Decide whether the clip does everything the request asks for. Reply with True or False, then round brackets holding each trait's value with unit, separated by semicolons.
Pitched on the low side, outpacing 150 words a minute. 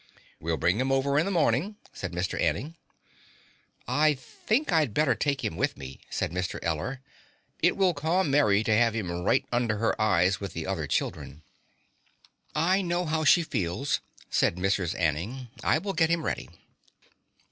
True (125 Hz; 170 wpm)